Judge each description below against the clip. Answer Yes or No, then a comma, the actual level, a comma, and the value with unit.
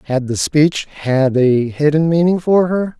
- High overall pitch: No, medium, 150 Hz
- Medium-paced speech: Yes, average, 180 wpm